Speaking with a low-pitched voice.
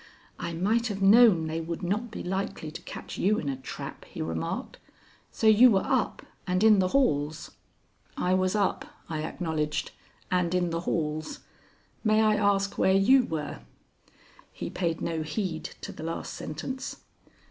No: medium, 185 Hz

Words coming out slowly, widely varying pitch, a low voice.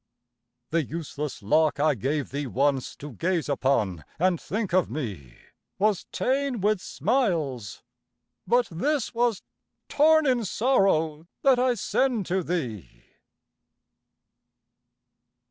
No: slow, 110 wpm; wide, 8.6 semitones; medium, 170 Hz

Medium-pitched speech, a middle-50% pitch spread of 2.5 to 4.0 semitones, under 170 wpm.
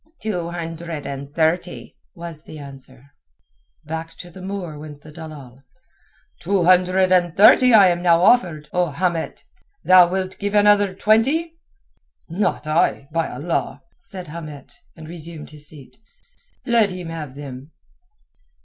Yes: medium, 170 Hz; average, 3.6 semitones; average, 140 wpm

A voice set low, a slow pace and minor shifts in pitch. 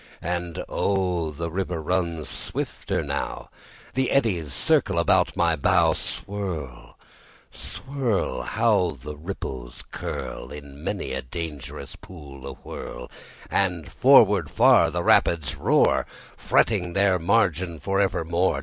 No: very low, 85 Hz; slow, 115 wpm; average, 4.5 semitones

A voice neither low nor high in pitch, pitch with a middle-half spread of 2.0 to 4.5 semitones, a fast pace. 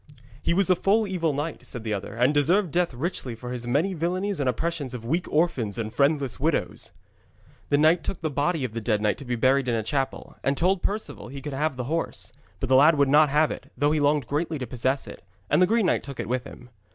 No: medium, 145 Hz; average, 4.9 semitones; fast, 250 wpm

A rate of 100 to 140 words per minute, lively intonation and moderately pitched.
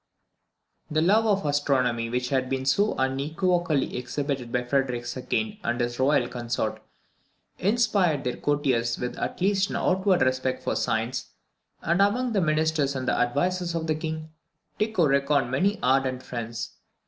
No: average, 150 wpm; wide, 5.9 semitones; medium, 145 Hz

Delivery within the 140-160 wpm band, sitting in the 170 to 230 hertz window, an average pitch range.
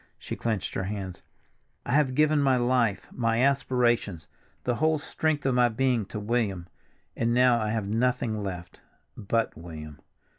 No: average, 150 wpm; low, 115 Hz; average, 4.0 semitones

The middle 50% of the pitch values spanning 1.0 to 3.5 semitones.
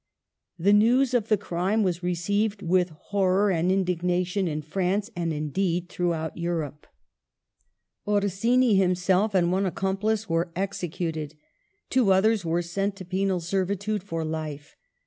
Yes: average, 2.9 semitones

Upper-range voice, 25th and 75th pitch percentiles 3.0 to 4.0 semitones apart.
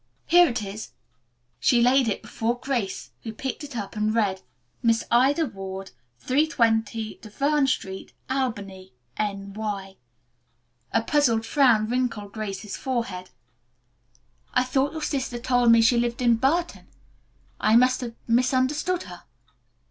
Yes: high, 235 Hz; average, 3.6 semitones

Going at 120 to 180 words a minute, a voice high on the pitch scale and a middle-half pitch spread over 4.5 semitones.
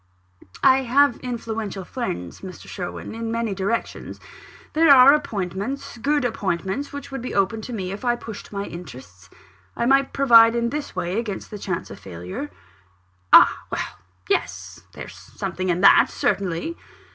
Yes: average, 155 wpm; high, 220 Hz; wide, 5.5 semitones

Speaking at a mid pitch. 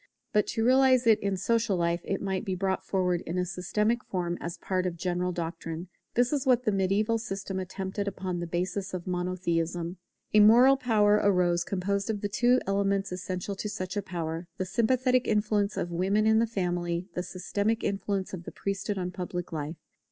No: high, 195 Hz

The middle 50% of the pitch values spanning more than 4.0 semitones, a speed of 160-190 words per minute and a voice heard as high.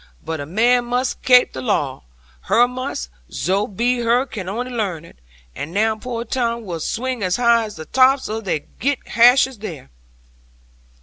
Yes: average, 5.2 semitones; average, 175 wpm; high, 230 Hz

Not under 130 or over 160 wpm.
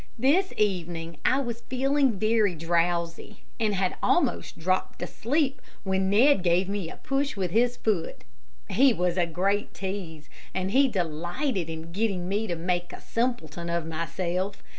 Yes: average, 155 wpm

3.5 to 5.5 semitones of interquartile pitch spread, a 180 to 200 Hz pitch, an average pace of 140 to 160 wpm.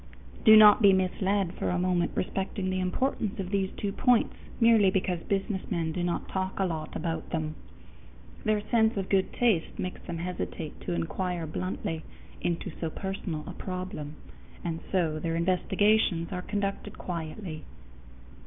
No: average, 2.9 semitones; medium, 185 Hz; average, 155 wpm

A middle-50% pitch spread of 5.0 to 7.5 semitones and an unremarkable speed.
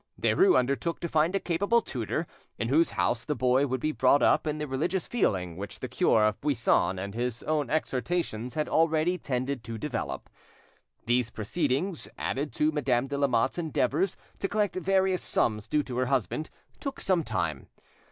Yes: wide, 5.4 semitones; average, 175 wpm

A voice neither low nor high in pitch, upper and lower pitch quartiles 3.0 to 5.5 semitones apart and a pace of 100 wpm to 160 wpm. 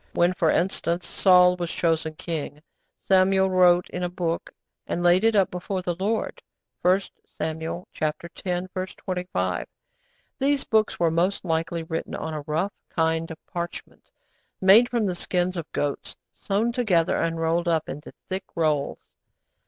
No: medium, 175 Hz; narrow, 2.4 semitones; average, 150 wpm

